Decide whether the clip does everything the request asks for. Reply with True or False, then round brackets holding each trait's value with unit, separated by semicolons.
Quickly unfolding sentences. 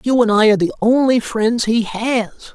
True (210 wpm)